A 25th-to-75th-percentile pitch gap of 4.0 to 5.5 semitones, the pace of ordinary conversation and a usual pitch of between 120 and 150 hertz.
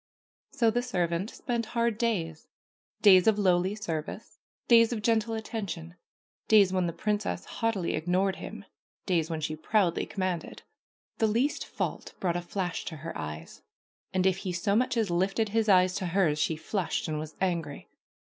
No: average, 4.3 semitones; average, 170 wpm; high, 190 Hz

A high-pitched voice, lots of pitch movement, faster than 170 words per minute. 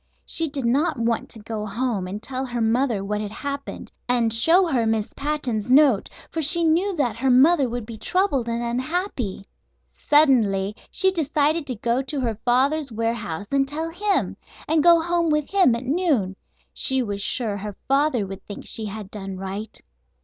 Yes: very high, 250 Hz; wide, 5.7 semitones; average, 180 wpm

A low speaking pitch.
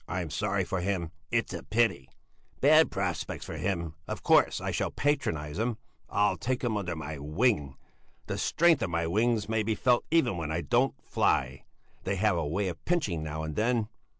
Yes: low, 100 Hz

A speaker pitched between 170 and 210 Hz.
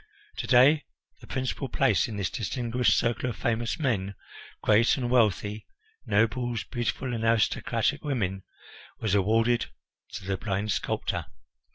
No: low, 115 Hz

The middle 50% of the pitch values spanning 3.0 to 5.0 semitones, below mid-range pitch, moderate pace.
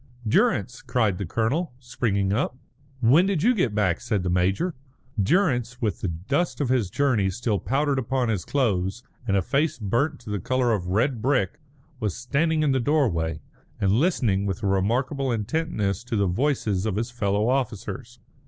No: wide, 5.5 semitones; low, 115 Hz; average, 175 wpm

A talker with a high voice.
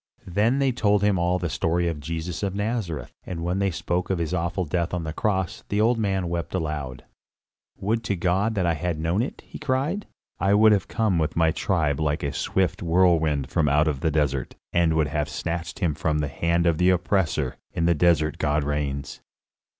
No: very low, 85 Hz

